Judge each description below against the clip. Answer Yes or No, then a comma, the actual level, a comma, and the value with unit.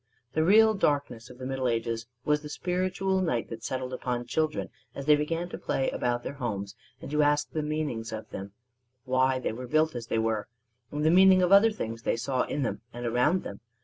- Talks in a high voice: No, low, 135 Hz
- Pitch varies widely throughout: No, average, 4.8 semitones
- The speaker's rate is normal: No, fast, 215 wpm